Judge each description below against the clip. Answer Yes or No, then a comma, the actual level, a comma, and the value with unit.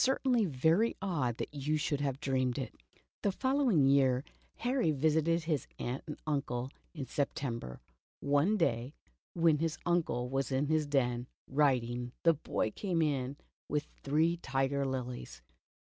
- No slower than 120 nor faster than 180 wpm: Yes, average, 145 wpm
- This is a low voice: No, medium, 145 Hz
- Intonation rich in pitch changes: No, average, 4.0 semitones